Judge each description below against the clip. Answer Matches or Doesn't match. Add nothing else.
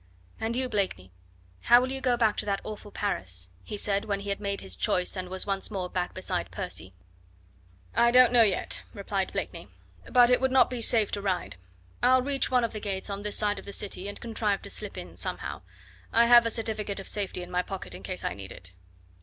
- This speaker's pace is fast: Matches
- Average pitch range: Matches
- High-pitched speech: Matches